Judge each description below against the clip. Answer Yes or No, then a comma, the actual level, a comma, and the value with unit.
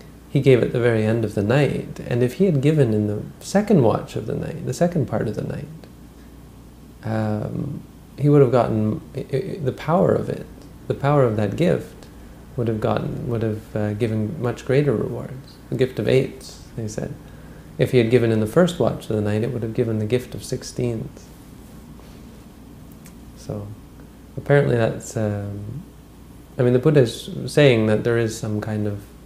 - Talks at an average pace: Yes, average, 195 wpm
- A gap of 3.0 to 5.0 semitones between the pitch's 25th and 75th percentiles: Yes, average, 4.2 semitones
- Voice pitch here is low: Yes, low, 120 Hz